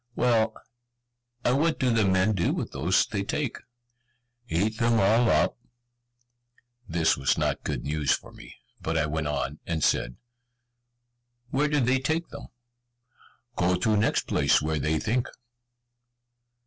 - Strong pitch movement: Yes, wide, 7.4 semitones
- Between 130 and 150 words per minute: Yes, average, 145 wpm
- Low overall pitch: Yes, low, 100 Hz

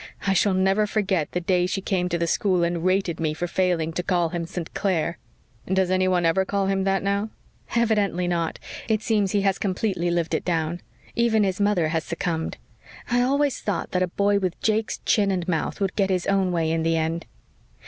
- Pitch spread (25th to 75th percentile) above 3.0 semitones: No, average, 2.7 semitones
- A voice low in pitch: No, medium, 185 Hz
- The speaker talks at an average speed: No, fast, 210 wpm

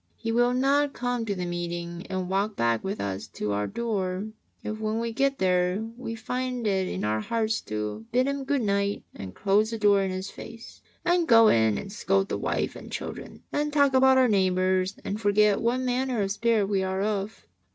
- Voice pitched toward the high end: Yes, high, 205 Hz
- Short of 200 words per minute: No, fast, 205 wpm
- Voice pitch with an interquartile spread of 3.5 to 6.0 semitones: Yes, average, 4.2 semitones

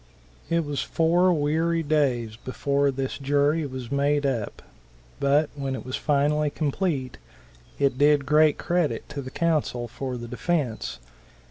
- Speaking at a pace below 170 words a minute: Yes, average, 140 wpm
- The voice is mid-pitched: Yes, medium, 145 Hz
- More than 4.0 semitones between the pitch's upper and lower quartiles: No, average, 2.7 semitones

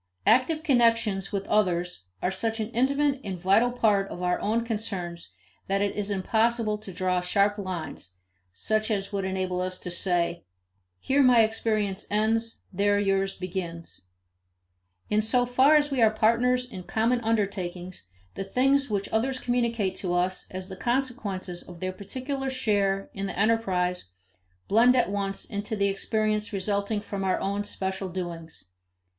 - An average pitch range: Yes, average, 3.5 semitones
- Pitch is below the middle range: No, high, 205 Hz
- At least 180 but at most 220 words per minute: No, average, 155 wpm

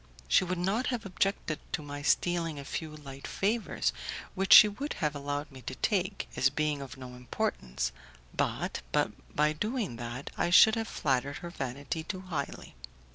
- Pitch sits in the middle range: Yes, medium, 155 Hz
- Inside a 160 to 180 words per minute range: Yes, average, 170 wpm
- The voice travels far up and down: Yes, wide, 5.7 semitones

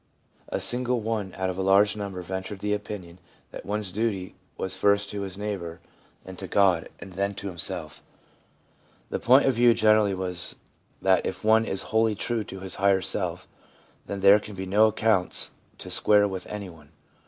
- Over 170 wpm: Yes, average, 185 wpm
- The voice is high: No, low, 100 Hz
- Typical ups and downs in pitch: No, narrow, 2.1 semitones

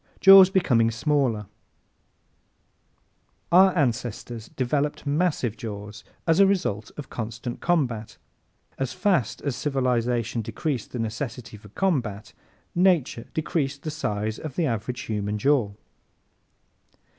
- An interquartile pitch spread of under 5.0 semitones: No, wide, 5.6 semitones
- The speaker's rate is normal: No, slow, 115 wpm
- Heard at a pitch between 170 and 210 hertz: No, low, 125 Hz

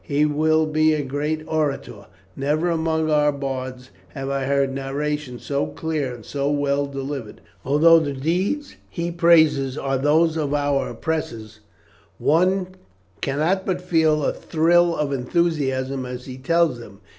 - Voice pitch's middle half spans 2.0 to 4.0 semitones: Yes, average, 2.9 semitones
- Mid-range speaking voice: Yes, medium, 145 Hz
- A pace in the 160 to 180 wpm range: No, average, 145 wpm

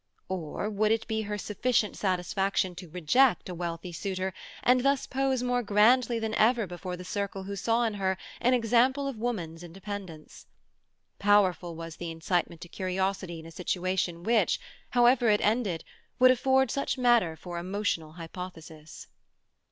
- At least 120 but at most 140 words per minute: No, average, 155 wpm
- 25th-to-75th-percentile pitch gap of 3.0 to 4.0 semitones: No, average, 4.9 semitones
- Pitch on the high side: Yes, high, 200 Hz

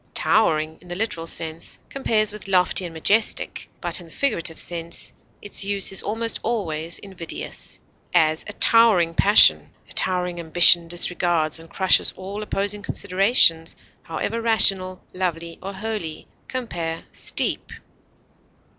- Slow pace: Yes, slow, 130 wpm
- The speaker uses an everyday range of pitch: Yes, average, 3.8 semitones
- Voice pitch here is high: No, medium, 180 Hz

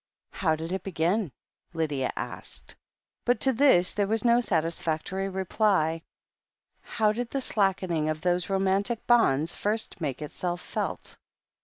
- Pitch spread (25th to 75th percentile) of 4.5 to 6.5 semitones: Yes, average, 4.9 semitones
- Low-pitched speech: No, high, 190 Hz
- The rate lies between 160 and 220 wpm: No, average, 140 wpm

